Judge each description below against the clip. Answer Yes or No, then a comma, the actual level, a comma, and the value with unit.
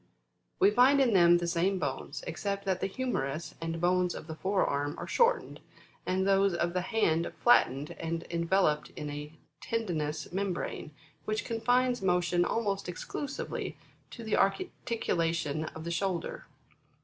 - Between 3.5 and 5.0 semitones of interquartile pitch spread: Yes, average, 4.1 semitones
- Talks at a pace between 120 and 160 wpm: Yes, average, 150 wpm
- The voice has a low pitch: No, medium, 180 Hz